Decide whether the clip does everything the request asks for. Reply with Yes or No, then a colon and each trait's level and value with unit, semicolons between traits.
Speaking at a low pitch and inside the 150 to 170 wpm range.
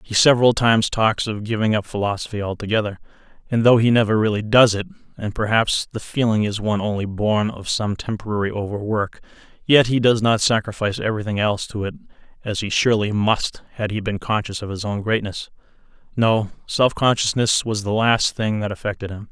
No: low, 110 Hz; average, 185 wpm